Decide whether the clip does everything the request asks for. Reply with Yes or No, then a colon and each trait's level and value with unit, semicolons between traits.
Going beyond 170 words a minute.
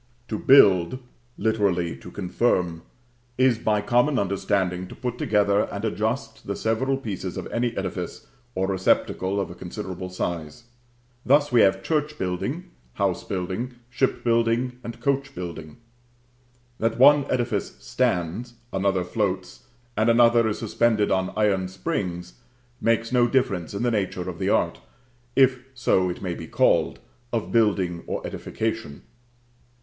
No: average, 140 wpm